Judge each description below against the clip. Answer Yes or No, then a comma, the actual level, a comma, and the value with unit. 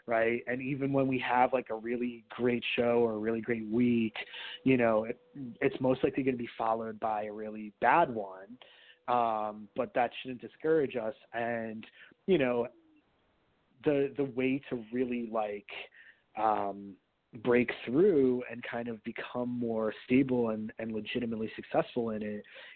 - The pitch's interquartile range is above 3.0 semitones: No, narrow, 2.5 semitones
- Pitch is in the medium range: No, low, 120 Hz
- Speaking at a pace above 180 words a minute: No, average, 160 wpm